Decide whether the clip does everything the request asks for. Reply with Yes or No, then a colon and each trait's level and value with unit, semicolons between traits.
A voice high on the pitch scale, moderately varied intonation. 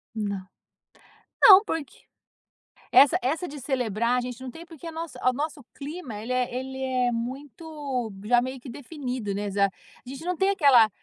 Yes: very high, 260 Hz; average, 3.8 semitones